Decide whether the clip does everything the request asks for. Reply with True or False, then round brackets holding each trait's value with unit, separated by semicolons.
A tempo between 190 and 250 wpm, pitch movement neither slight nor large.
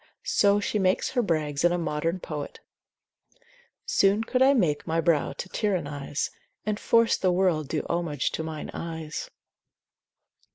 False (150 wpm; 4.7 semitones)